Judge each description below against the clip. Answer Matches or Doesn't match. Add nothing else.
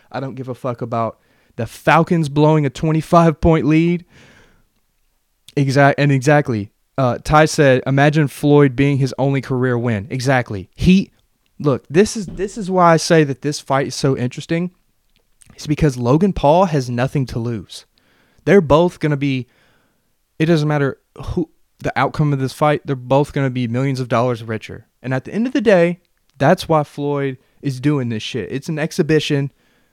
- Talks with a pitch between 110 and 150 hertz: Matches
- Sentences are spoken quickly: Doesn't match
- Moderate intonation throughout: Matches